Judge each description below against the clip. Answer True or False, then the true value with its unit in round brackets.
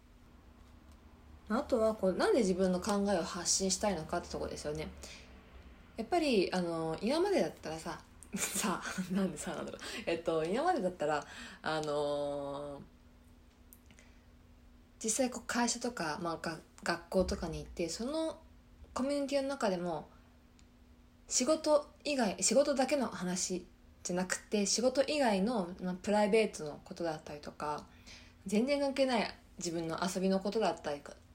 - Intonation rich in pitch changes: True (7.7 semitones)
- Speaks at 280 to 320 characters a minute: True (295 characters per minute)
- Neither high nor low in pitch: True (180 Hz)